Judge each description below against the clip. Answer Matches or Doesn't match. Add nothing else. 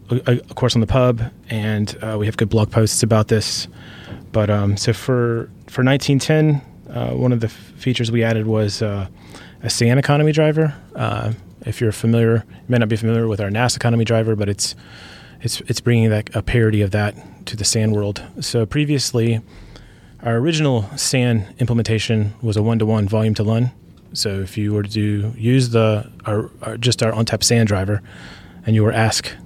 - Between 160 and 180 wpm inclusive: Doesn't match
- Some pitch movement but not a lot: Doesn't match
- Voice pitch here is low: Matches